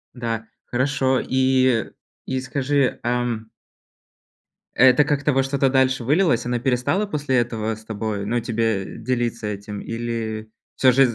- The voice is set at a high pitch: No, low, 125 Hz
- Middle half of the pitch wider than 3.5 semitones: No, average, 2.8 semitones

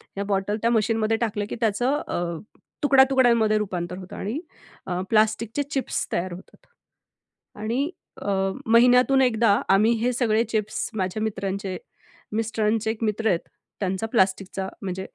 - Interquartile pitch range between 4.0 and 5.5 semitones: No, average, 3.1 semitones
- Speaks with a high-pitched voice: Yes, high, 215 Hz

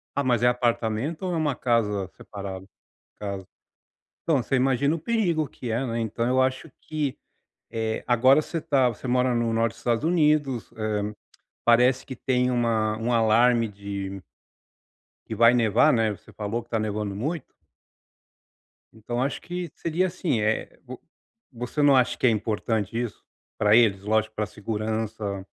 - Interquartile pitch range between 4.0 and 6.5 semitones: No, average, 3.3 semitones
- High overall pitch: No, low, 120 Hz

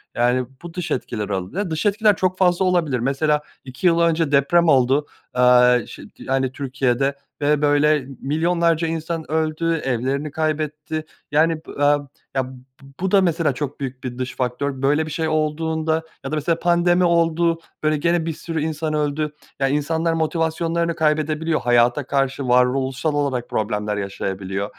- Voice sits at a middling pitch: Yes, medium, 150 Hz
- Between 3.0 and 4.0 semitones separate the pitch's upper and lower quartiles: Yes, average, 3.7 semitones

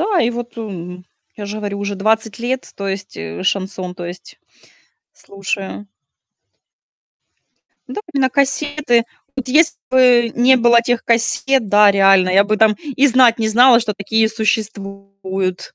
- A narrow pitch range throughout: No, average, 3.7 semitones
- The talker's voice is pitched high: Yes, high, 220 Hz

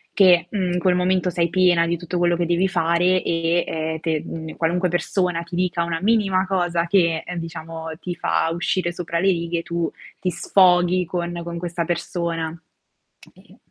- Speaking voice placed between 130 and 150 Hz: No, medium, 175 Hz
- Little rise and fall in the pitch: Yes, narrow, 1.3 semitones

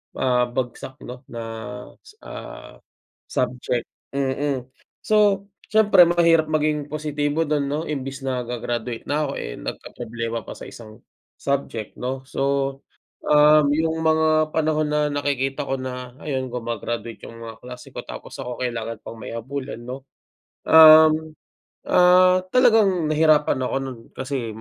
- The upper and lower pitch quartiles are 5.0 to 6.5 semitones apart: No, average, 4.0 semitones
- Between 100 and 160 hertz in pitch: Yes, medium, 140 Hz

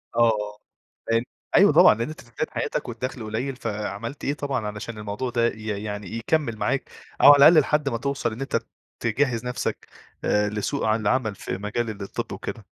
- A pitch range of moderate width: Yes, average, 3.3 semitones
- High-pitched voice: No, low, 115 Hz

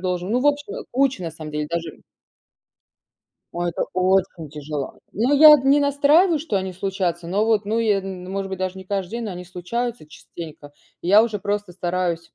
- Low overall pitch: No, high, 190 Hz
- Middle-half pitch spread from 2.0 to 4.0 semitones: No, average, 5.1 semitones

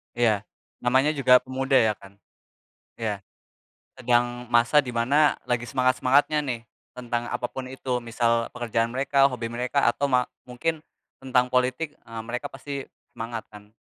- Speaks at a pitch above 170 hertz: No, low, 125 Hz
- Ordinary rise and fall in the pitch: No, narrow, 2.1 semitones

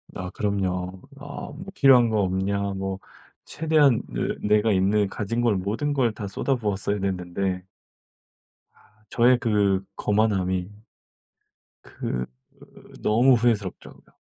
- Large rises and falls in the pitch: No, average, 3.6 semitones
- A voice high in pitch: No, low, 105 Hz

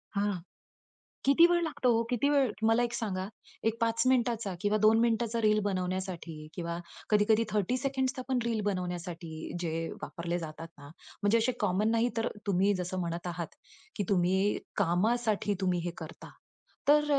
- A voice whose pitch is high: Yes, high, 205 Hz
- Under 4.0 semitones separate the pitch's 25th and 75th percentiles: No, average, 4.7 semitones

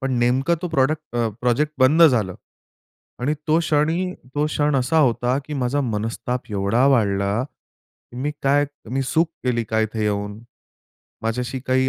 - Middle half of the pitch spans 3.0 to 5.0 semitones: Yes, average, 4.6 semitones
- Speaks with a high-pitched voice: No, low, 130 Hz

